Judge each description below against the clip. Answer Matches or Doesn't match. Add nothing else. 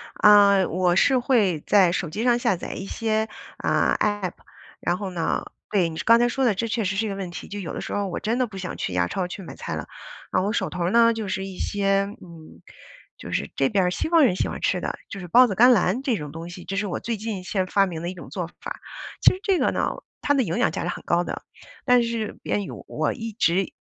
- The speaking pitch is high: Matches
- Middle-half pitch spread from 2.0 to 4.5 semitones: Matches